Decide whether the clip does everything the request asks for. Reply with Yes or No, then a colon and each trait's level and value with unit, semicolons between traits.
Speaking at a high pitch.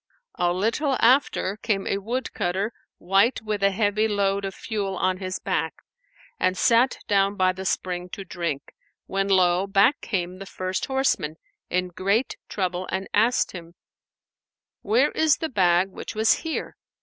Yes: high, 195 Hz